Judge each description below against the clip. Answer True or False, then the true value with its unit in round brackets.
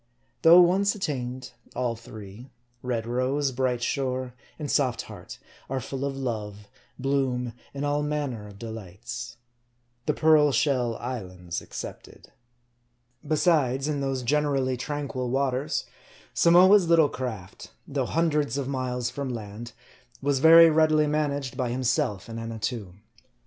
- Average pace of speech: False (130 wpm)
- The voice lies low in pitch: True (130 Hz)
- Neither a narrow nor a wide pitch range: True (3.6 semitones)